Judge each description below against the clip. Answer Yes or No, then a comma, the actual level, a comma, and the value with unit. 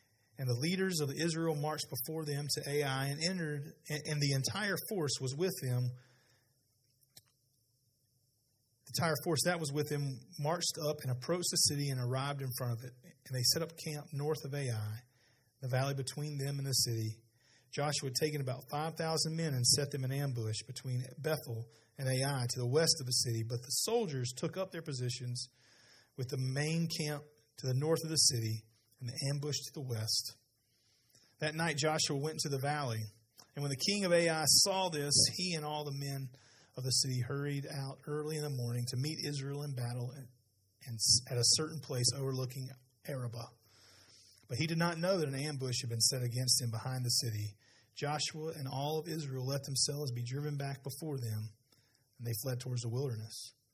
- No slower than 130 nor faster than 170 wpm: No, average, 190 wpm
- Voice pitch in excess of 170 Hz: No, low, 135 Hz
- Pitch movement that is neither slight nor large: Yes, average, 3.4 semitones